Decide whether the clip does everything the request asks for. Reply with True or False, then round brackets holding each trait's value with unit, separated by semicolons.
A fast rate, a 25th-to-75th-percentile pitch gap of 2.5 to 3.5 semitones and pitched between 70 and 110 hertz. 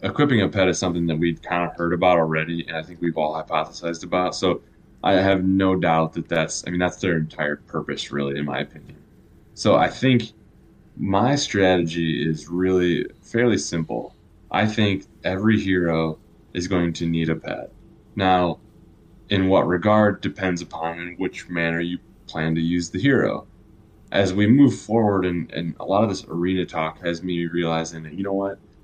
False (185 wpm; 2.9 semitones; 90 Hz)